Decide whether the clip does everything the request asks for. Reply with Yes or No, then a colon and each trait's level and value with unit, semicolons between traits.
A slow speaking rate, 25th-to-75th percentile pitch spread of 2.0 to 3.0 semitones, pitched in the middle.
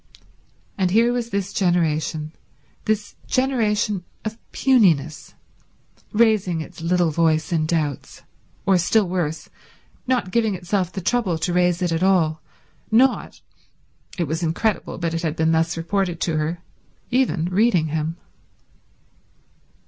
No: slow, 125 wpm; average, 4.5 semitones; medium, 180 Hz